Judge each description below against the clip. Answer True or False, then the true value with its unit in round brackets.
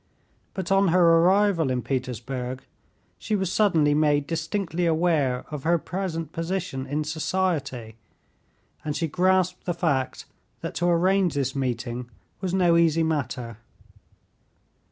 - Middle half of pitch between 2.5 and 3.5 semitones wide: False (5.0 semitones)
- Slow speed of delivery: True (130 wpm)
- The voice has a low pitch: False (165 Hz)